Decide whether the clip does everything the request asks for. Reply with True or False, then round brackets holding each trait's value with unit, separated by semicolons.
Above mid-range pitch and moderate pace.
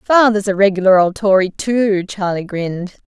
True (195 Hz; 155 wpm)